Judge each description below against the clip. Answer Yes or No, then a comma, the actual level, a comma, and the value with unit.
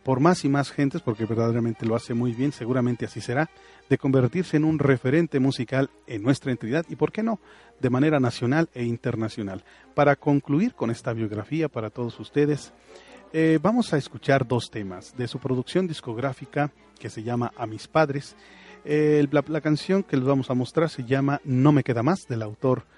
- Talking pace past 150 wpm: Yes, fast, 190 wpm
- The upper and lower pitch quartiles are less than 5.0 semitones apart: Yes, average, 4.0 semitones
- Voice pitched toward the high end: No, low, 135 Hz